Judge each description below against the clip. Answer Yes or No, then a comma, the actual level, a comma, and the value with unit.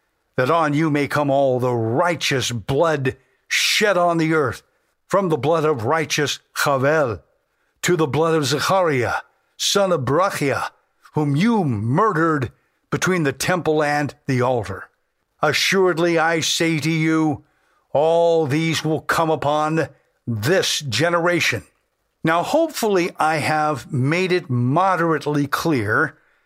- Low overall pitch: No, medium, 155 Hz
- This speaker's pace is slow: Yes, slow, 125 wpm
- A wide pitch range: No, average, 3.3 semitones